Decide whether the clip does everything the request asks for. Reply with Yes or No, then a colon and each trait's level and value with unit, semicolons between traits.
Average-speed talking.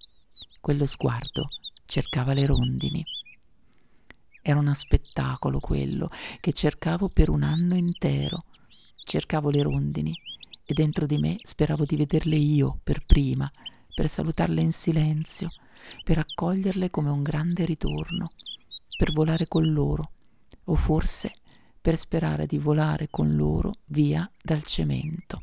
Yes: average, 125 wpm